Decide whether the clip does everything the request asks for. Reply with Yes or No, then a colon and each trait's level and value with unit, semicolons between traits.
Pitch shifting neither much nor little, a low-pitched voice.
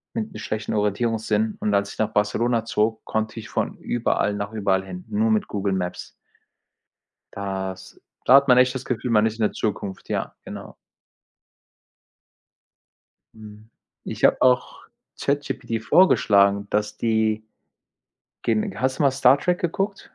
Yes: average, 3.6 semitones; low, 110 Hz